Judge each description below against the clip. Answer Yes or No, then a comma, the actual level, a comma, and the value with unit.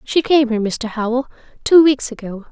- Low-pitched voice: No, very high, 250 Hz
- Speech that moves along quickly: No, average, 190 wpm